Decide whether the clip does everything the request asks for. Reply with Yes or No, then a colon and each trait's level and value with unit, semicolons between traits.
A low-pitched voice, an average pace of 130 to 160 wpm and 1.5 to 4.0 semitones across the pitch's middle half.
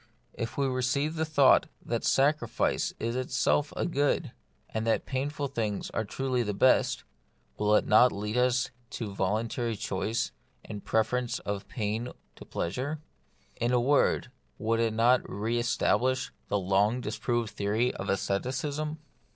Yes: low, 120 Hz; average, 145 wpm; average, 3.4 semitones